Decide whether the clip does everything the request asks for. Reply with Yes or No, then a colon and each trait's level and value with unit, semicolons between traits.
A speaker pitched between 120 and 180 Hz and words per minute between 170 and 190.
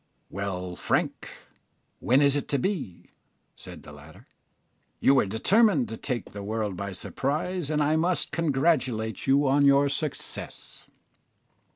No: low, 135 Hz; average, 140 wpm